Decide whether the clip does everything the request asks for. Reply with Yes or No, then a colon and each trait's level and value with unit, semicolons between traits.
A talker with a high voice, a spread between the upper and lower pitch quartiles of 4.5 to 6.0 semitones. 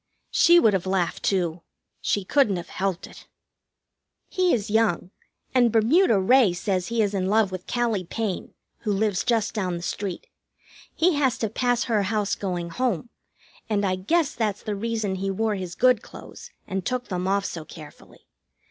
No: high, 205 Hz; average, 3.8 semitones